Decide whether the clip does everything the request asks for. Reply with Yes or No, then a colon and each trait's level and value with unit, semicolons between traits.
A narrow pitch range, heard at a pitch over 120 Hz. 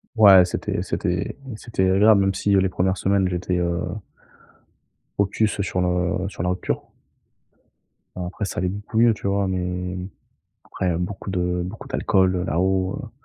No: narrow, 1.8 semitones; very low, 95 Hz